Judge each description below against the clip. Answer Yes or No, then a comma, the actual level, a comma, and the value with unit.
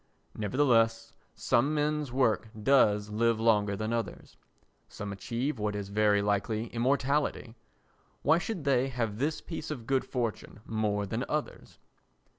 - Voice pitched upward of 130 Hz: No, low, 115 Hz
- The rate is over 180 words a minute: No, slow, 135 wpm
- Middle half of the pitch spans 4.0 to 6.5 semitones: Yes, average, 4.5 semitones